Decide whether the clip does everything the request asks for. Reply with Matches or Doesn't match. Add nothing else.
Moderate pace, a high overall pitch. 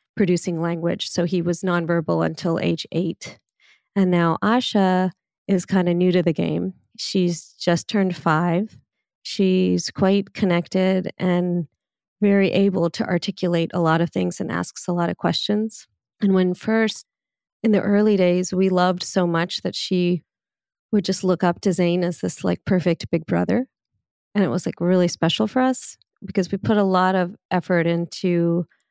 Doesn't match